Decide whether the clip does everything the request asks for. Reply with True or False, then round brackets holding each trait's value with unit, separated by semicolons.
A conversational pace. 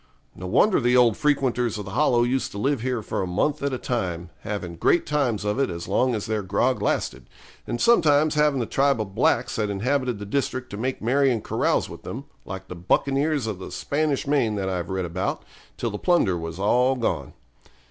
False (215 wpm)